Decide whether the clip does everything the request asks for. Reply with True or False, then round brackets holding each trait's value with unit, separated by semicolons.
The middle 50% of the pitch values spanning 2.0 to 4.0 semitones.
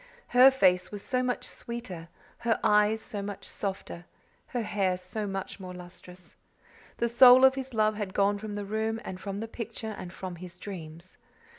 True (3.5 semitones)